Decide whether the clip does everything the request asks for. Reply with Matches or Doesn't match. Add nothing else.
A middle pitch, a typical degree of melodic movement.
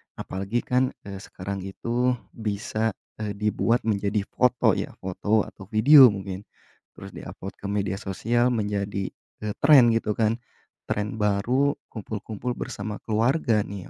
Doesn't match